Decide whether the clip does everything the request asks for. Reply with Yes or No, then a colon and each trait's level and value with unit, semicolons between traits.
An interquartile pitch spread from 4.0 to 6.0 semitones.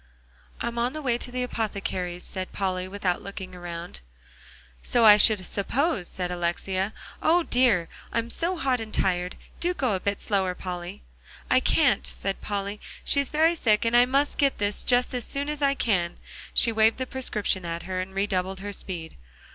Yes: average, 5.2 semitones